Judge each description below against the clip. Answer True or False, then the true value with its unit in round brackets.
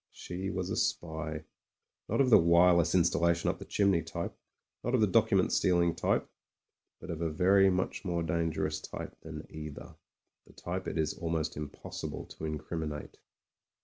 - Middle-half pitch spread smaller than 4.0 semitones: True (2.4 semitones)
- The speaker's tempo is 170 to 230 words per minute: True (175 wpm)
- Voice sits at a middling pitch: False (85 Hz)